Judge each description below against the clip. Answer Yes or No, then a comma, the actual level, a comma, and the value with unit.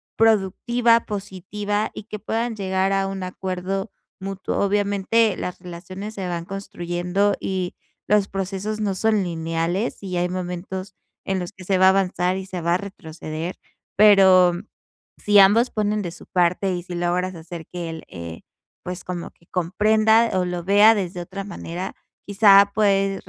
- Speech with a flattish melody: Yes, narrow, 2.3 semitones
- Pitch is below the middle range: No, high, 190 Hz